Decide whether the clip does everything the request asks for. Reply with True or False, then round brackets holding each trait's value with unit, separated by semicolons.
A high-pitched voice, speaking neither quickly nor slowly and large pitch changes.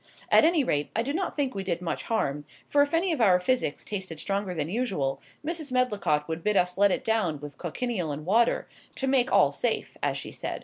False (200 Hz; 225 wpm; 7.5 semitones)